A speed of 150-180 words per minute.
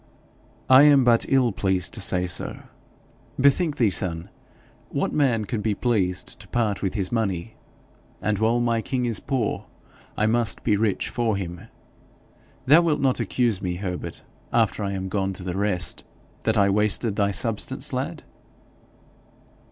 Yes: average, 160 wpm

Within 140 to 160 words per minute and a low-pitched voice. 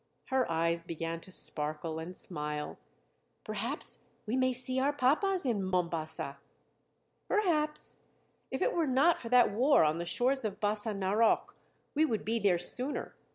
No: average, 155 wpm; high, 215 Hz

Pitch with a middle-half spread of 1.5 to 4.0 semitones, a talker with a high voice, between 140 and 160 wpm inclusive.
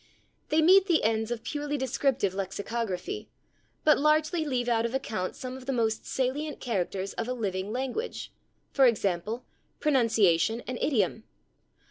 No: average, 4.7 semitones; high, 240 Hz; average, 150 wpm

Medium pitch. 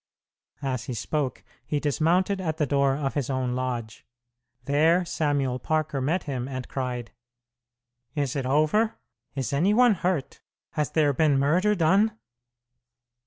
Yes: medium, 145 Hz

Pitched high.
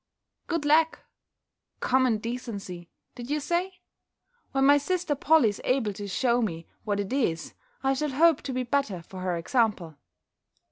Yes: very high, 250 Hz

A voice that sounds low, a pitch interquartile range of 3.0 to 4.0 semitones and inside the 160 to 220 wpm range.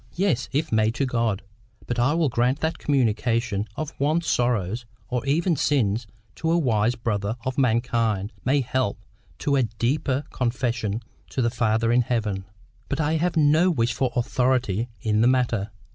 Yes: low, 125 Hz; average, 3.6 semitones; average, 165 wpm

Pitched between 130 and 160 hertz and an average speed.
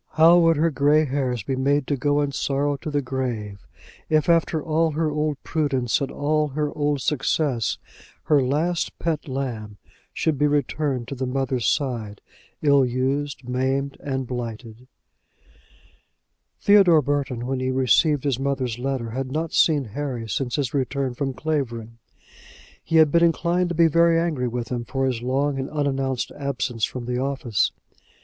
Yes: medium, 140 Hz; average, 165 wpm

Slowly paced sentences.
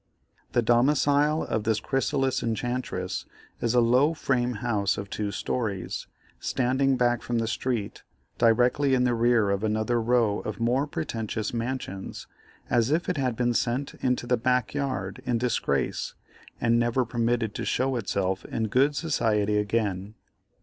No: average, 150 wpm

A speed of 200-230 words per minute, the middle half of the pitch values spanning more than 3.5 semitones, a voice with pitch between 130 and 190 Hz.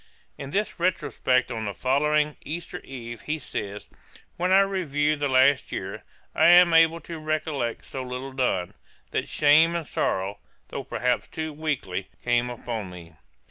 No: average, 155 wpm; average, 4.7 semitones; medium, 140 Hz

